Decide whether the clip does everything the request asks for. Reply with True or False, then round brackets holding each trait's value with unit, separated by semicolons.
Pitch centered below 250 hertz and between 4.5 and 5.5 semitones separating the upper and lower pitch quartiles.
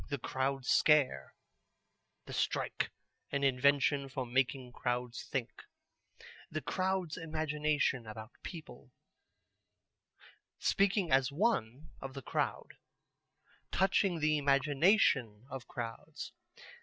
False (140 Hz; 3.7 semitones)